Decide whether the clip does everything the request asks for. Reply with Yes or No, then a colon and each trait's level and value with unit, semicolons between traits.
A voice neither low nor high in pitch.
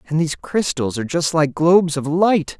Yes: medium, 160 Hz